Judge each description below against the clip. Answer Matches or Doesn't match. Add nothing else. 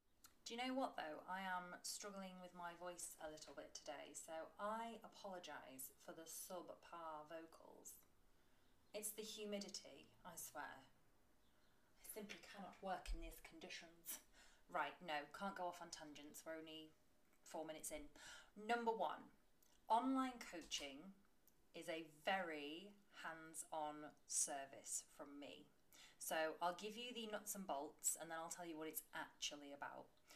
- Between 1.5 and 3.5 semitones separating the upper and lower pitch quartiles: Doesn't match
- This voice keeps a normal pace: Matches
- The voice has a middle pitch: Matches